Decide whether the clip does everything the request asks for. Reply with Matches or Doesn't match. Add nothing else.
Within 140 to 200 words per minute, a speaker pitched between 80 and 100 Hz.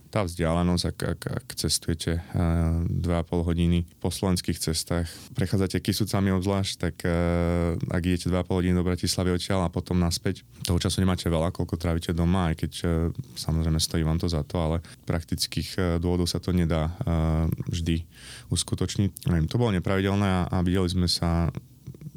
Matches